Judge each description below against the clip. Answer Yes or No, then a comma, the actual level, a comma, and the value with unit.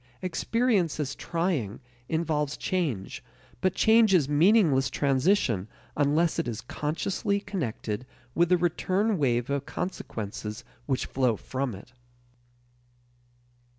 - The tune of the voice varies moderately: No, wide, 6.5 semitones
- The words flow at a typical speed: No, slow, 110 wpm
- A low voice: No, medium, 150 Hz